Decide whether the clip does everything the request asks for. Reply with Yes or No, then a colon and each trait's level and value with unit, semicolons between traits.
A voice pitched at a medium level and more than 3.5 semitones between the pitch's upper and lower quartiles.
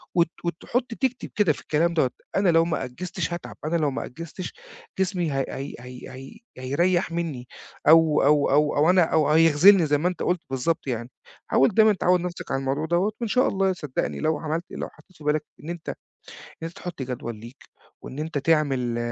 Yes: medium, 160 Hz; average, 4.1 semitones